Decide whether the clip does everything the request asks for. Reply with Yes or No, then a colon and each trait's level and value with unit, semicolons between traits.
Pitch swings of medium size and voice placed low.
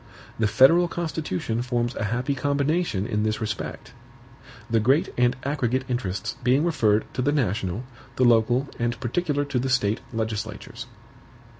Yes: average, 4.1 semitones; low, 120 Hz